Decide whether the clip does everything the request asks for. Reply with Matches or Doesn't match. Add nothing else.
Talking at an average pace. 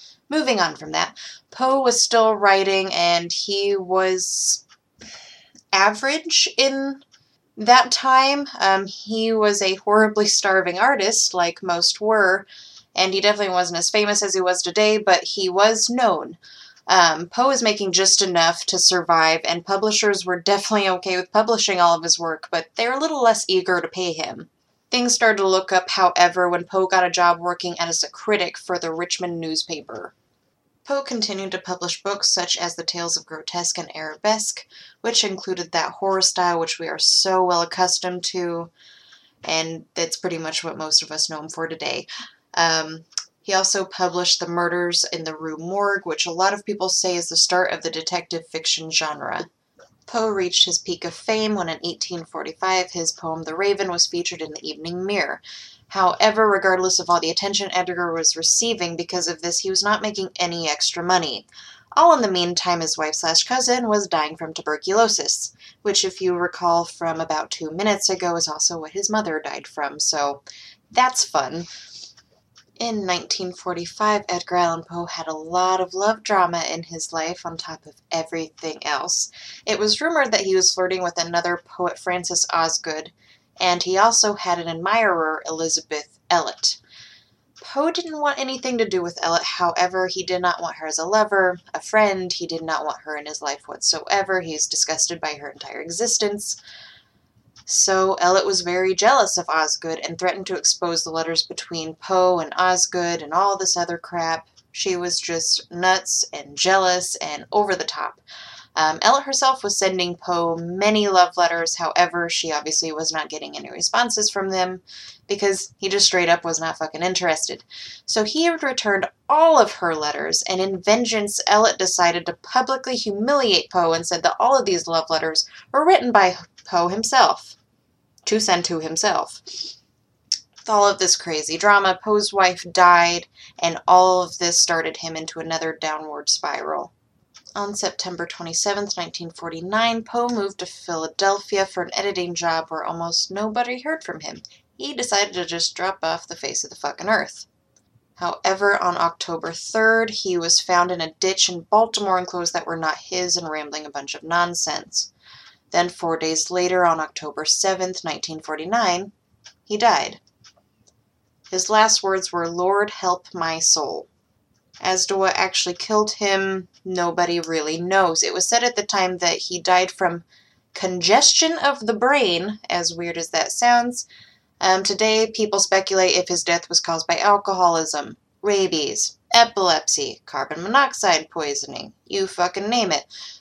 Matches